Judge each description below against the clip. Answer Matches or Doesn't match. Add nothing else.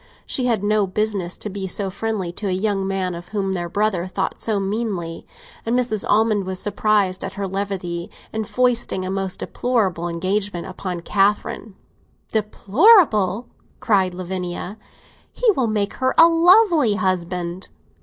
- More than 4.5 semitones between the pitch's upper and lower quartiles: Doesn't match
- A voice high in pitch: Matches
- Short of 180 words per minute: Matches